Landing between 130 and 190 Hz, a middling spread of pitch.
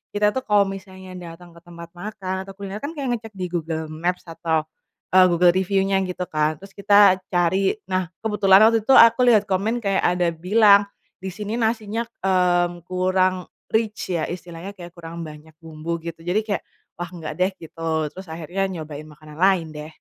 Yes: medium, 185 Hz; average, 3.0 semitones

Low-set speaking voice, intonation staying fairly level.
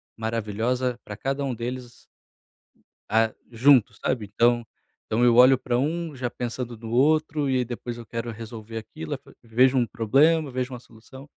Yes: low, 120 Hz; narrow, 2.3 semitones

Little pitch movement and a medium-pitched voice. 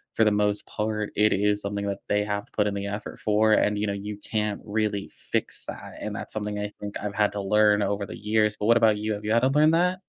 No: narrow, 0.8 semitones; low, 105 Hz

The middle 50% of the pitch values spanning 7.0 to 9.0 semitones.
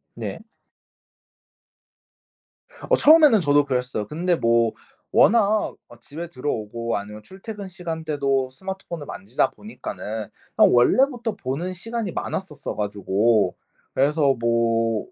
Yes: wide, 8.5 semitones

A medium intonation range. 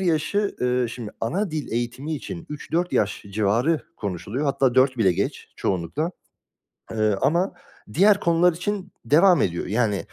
No: wide, 7.3 semitones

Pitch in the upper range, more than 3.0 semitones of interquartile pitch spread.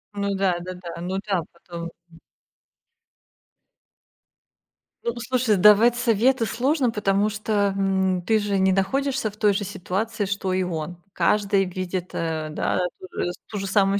No: high, 195 Hz; narrow, 2.6 semitones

